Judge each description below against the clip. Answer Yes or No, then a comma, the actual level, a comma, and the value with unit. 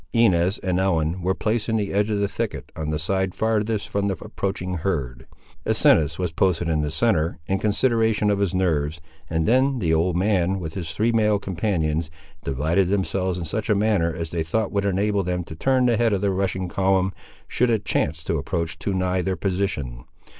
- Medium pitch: No, very low, 95 Hz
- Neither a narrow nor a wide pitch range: Yes, average, 3.8 semitones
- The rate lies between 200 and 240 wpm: Yes, fast, 205 wpm